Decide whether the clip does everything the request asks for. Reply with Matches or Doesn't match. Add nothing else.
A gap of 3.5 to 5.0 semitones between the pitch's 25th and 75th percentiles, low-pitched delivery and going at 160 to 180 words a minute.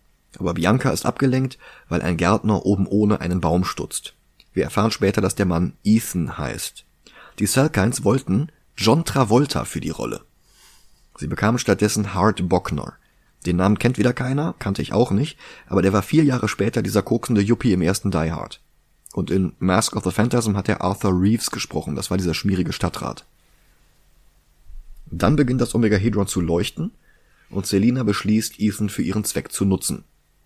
Matches